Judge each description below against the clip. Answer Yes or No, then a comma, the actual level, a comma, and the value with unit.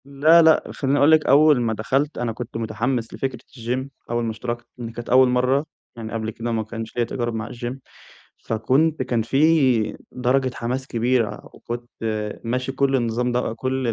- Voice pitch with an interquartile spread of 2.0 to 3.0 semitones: Yes, narrow, 2.6 semitones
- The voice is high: No, low, 125 Hz